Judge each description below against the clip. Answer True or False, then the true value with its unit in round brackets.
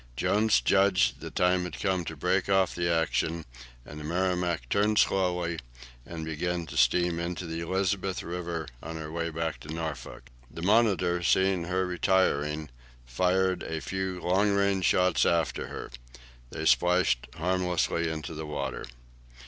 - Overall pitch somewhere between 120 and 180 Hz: False (90 Hz)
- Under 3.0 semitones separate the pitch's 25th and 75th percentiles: True (2.4 semitones)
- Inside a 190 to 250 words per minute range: False (150 wpm)